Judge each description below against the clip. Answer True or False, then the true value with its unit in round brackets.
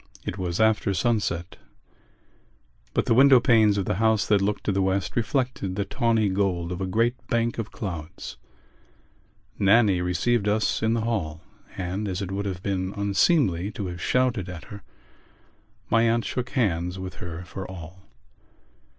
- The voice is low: True (100 Hz)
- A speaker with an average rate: True (165 wpm)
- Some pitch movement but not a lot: True (3.7 semitones)